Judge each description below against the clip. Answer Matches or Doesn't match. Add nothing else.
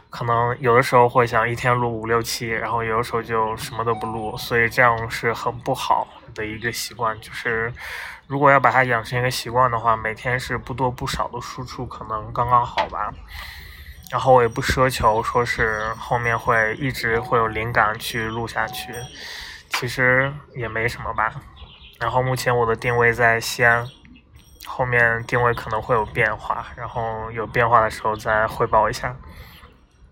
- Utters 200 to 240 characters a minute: Doesn't match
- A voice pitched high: Doesn't match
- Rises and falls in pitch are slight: Matches